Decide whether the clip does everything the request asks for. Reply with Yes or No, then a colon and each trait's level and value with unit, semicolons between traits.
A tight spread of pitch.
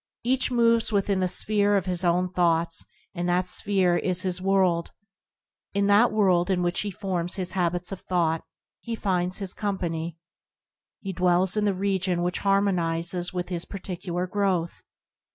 Yes: narrow, 2.1 semitones